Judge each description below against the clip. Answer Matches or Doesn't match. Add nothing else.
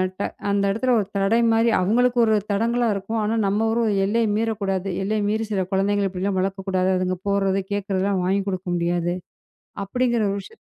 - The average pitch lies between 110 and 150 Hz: Doesn't match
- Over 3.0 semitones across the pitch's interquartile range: Doesn't match